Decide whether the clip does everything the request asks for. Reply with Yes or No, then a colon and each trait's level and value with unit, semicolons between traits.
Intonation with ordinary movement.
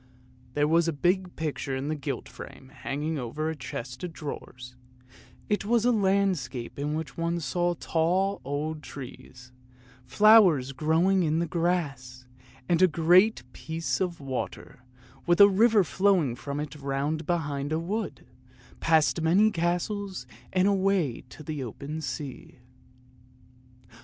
Yes: average, 4.6 semitones